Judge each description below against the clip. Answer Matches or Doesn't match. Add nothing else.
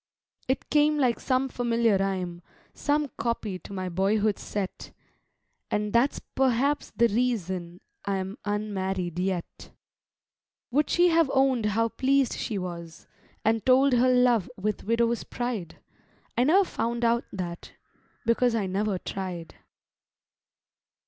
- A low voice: Doesn't match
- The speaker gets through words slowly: Matches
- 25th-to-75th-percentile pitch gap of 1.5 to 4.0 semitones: Doesn't match